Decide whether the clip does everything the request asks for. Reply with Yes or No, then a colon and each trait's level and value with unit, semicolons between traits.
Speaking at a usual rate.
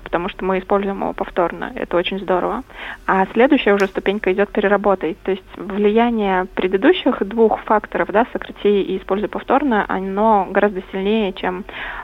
Yes: average, 150 wpm